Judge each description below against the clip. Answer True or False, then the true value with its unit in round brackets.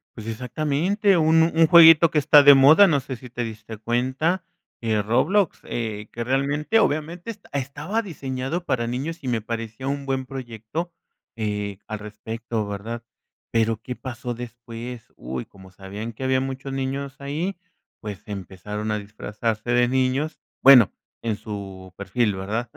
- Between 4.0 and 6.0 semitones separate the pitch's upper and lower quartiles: True (4.6 semitones)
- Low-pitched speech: True (125 Hz)